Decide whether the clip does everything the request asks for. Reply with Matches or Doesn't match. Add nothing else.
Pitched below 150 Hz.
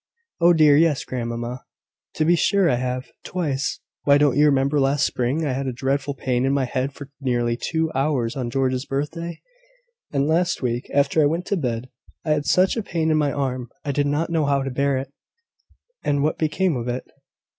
Matches